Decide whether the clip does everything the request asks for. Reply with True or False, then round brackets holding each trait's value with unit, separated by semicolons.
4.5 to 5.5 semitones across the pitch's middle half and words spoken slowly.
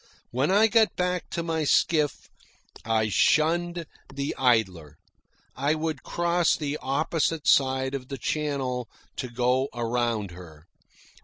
True (5.1 semitones; 130 wpm)